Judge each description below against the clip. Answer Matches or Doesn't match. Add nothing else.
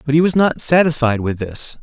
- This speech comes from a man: Matches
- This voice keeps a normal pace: Doesn't match